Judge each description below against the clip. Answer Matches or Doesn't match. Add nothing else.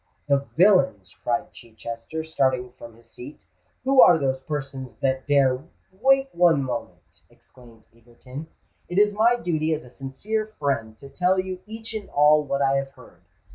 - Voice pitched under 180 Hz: Matches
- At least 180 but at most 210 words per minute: Doesn't match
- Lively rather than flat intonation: Matches